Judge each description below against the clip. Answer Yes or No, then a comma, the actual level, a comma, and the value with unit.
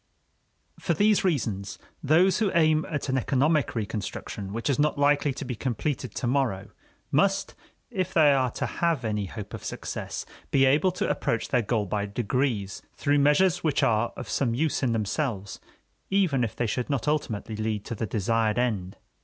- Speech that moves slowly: No, average, 180 wpm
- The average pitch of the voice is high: No, low, 130 Hz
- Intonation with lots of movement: Yes, wide, 5.7 semitones